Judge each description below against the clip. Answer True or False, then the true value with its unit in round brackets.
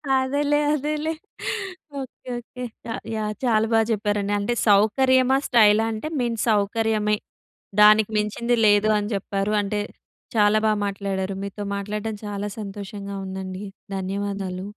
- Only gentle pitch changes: True (2.2 semitones)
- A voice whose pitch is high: True (210 Hz)